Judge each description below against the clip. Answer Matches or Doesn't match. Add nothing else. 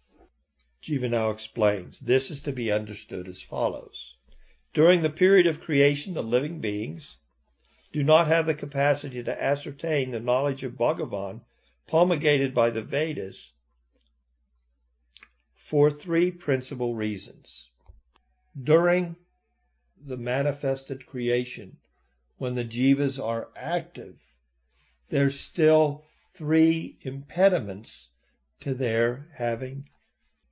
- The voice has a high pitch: Doesn't match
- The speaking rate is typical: Doesn't match